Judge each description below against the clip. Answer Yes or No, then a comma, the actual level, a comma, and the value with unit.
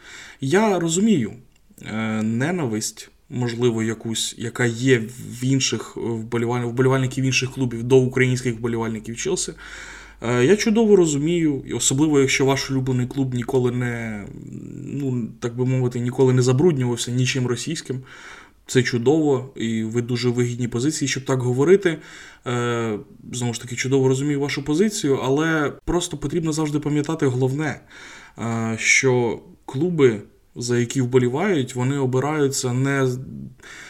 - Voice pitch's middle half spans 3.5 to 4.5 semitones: No, average, 2.9 semitones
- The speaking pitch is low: Yes, low, 130 Hz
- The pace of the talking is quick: No, average, 120 wpm